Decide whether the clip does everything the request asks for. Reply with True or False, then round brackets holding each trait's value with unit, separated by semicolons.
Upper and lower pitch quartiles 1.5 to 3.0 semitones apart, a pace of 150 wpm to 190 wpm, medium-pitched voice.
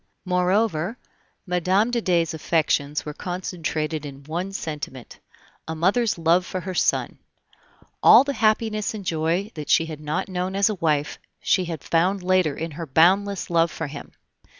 False (3.5 semitones; 160 wpm; 175 Hz)